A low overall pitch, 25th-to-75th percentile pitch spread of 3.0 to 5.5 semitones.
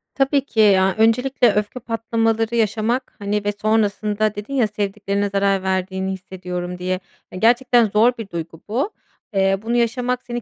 No: high, 215 Hz; average, 3.3 semitones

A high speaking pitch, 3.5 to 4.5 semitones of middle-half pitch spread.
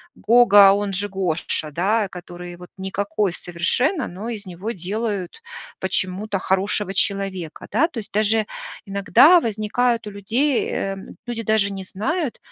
No: high, 200 Hz; average, 2.9 semitones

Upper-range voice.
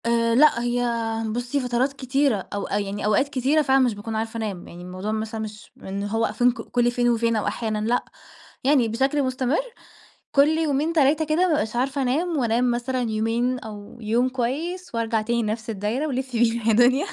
Yes: high, 240 Hz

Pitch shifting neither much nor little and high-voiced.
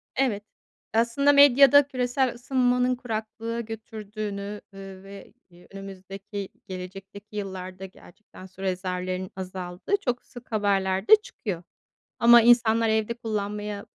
Yes: average, 3.6 semitones; high, 210 Hz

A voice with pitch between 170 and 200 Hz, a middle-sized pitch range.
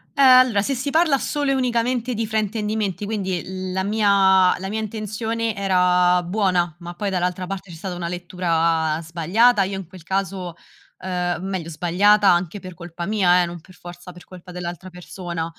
Yes: medium, 185 Hz; average, 3.3 semitones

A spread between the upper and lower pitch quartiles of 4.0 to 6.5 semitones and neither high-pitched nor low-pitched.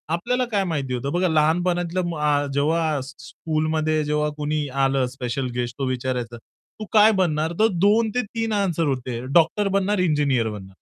Yes: average, 5.1 semitones; medium, 155 Hz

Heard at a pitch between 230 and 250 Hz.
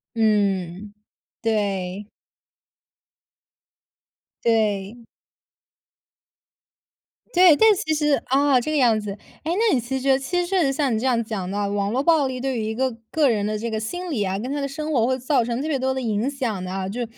Yes: high, 240 Hz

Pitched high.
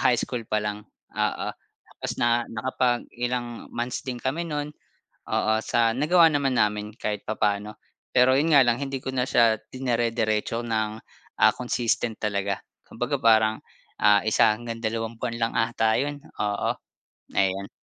No: low, 115 Hz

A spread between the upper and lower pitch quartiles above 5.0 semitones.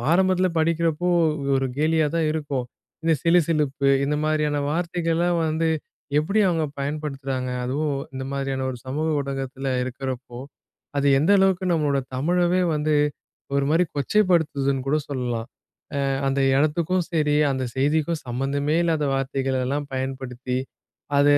No: average, 3.4 semitones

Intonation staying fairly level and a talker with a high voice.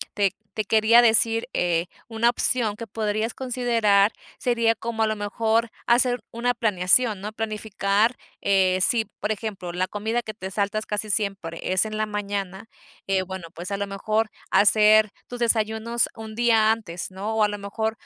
Yes: narrow, 2.2 semitones; high, 215 Hz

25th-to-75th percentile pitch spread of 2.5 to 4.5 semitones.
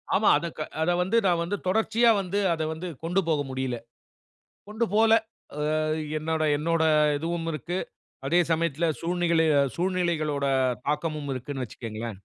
Yes: average, 3.3 semitones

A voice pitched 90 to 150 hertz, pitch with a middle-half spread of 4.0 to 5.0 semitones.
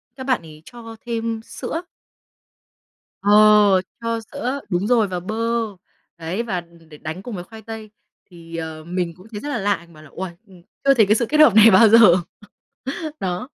No: high, 205 Hz; average, 4.7 semitones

